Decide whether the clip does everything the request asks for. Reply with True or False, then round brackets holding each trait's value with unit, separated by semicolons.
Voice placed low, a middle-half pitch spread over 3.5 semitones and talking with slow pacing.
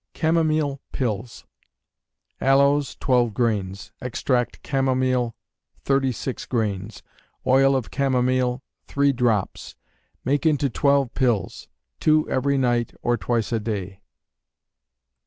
False (130 Hz; 2.9 semitones; 100 wpm)